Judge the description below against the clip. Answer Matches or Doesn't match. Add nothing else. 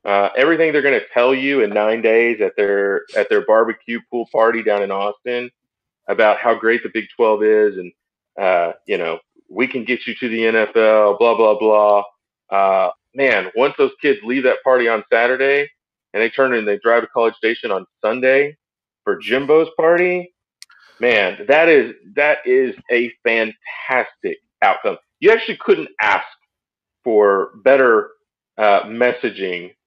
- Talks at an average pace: Matches